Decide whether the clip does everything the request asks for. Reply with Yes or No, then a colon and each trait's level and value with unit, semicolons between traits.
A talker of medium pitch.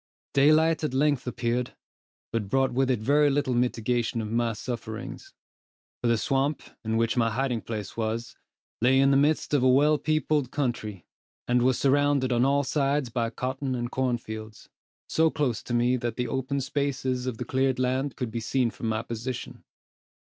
No: low, 125 Hz